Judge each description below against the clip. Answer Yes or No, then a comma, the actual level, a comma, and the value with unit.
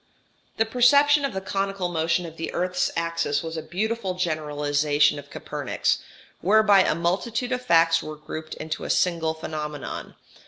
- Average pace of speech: Yes, average, 160 wpm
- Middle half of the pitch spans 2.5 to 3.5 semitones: No, average, 4.1 semitones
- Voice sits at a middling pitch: Yes, medium, 170 Hz